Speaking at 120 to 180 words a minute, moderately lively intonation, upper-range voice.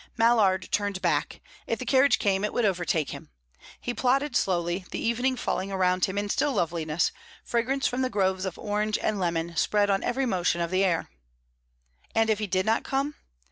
No: average, 190 wpm; average, 4.3 semitones; high, 205 Hz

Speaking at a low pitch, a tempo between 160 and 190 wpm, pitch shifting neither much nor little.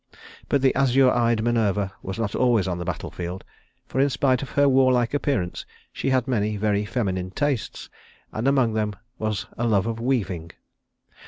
Yes: low, 115 Hz; average, 175 wpm; average, 4.4 semitones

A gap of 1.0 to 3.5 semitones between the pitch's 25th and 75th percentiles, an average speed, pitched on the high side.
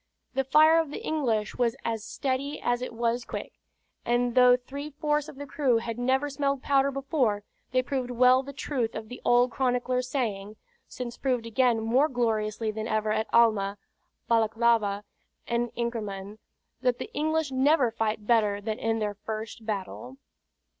Yes: average, 3.2 semitones; average, 165 wpm; high, 240 Hz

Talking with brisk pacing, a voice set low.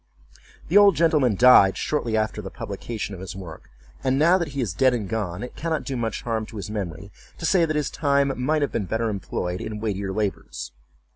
Yes: fast, 215 wpm; low, 115 Hz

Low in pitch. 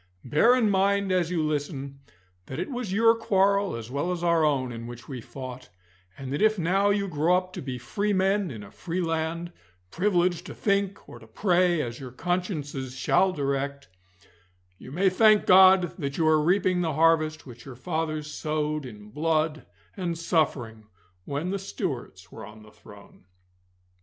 No: medium, 160 Hz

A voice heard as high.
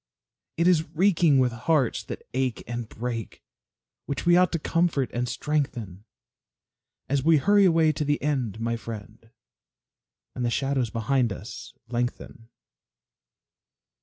No: low, 130 Hz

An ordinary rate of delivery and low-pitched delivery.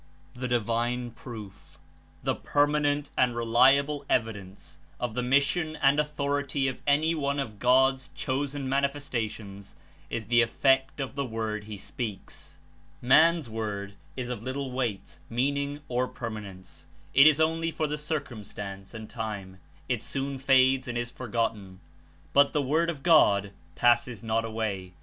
Yes: average, 145 wpm; low, 125 Hz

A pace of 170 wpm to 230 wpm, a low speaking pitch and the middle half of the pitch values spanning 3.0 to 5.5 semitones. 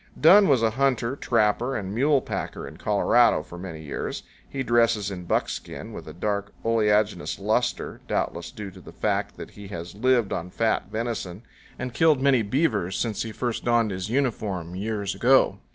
Yes: average, 175 wpm; low, 110 Hz; average, 4.2 semitones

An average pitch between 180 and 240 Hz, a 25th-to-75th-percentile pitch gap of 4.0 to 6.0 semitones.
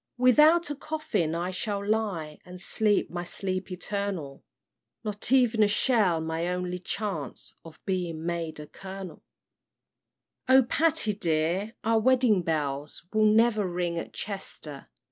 Yes: high, 190 Hz; average, 4.5 semitones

